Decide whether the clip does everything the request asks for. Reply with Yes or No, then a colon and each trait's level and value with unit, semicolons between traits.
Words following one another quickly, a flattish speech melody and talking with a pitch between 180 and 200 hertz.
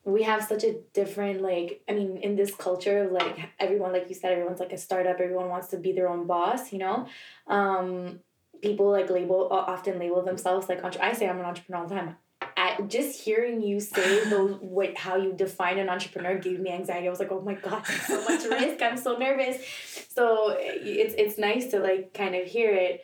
Yes: fast, 220 wpm; narrow, 2.2 semitones; high, 190 Hz